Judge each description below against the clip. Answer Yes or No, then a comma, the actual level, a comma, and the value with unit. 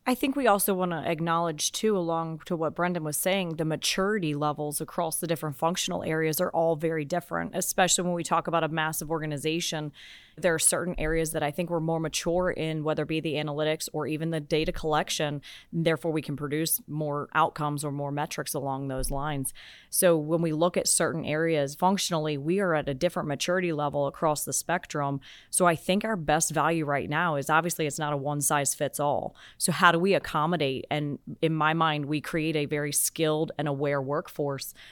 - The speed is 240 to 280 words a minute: No, fast, 205 wpm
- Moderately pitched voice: Yes, medium, 160 Hz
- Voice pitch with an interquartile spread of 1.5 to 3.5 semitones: Yes, narrow, 2.4 semitones